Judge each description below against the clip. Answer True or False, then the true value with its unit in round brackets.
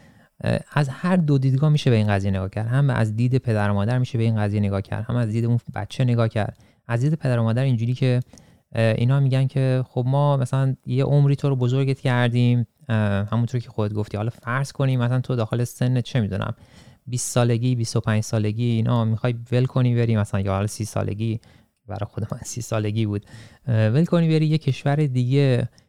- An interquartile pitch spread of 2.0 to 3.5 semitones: True (2.9 semitones)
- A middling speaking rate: False (200 wpm)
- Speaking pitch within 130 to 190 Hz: False (120 Hz)